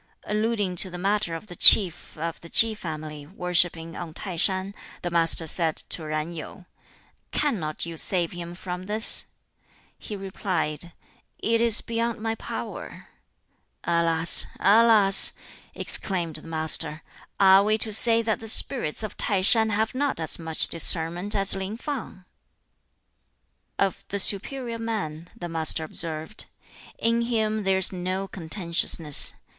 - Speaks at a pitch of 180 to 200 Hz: Yes, medium, 185 Hz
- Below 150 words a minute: Yes, average, 140 wpm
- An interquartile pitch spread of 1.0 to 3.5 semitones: No, average, 4.5 semitones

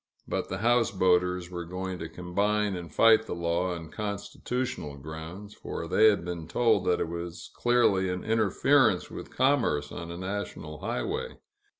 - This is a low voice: Yes, very low, 90 Hz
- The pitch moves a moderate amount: Yes, average, 4.0 semitones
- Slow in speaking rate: No, average, 160 wpm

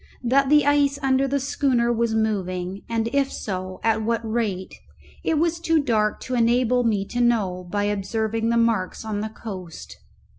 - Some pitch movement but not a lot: Yes, average, 3.8 semitones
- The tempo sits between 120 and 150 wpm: No, average, 175 wpm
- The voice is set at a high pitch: Yes, high, 230 Hz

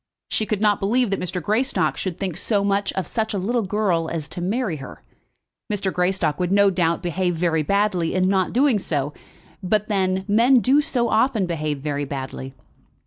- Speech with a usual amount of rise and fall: Yes, average, 4.0 semitones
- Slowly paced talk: No, average, 190 wpm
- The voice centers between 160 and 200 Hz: Yes, high, 190 Hz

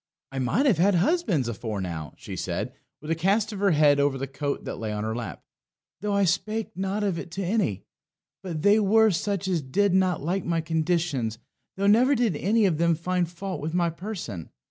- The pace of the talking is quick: Yes, fast, 210 wpm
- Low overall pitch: No, medium, 175 Hz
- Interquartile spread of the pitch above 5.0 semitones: Yes, wide, 5.6 semitones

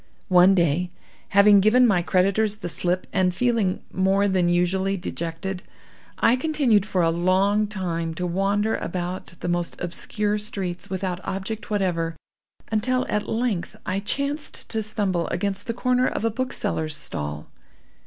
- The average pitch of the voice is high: Yes, high, 195 Hz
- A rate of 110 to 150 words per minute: Yes, average, 145 wpm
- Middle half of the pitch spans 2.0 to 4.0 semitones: Yes, average, 3.2 semitones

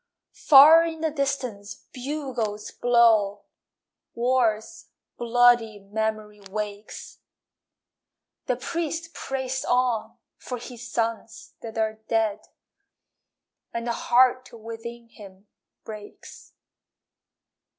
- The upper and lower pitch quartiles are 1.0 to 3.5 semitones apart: Yes, average, 2.9 semitones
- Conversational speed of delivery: No, slow, 90 wpm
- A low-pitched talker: No, high, 235 Hz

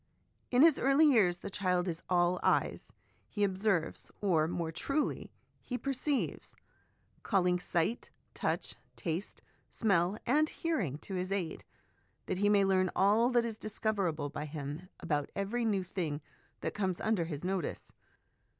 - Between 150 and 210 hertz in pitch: Yes, high, 190 Hz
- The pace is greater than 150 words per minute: No, average, 145 wpm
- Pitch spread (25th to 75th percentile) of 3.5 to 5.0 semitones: Yes, average, 4.2 semitones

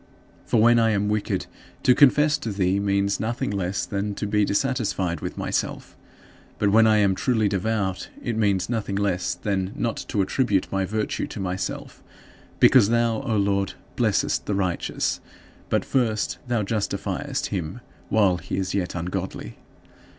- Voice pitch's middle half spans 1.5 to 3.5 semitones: Yes, narrow, 2.6 semitones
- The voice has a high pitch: No, low, 100 Hz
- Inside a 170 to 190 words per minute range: No, average, 160 wpm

